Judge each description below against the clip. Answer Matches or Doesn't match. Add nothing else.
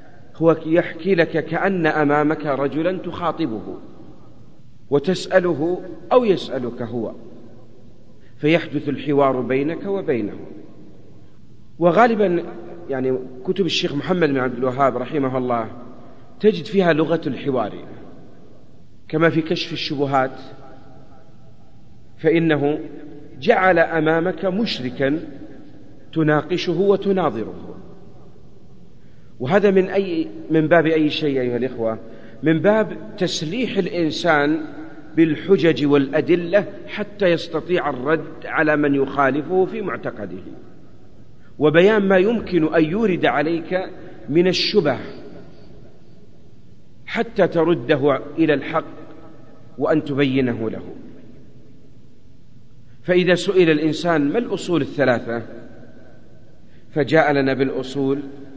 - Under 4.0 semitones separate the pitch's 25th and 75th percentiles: Doesn't match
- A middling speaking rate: Matches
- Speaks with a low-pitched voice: Doesn't match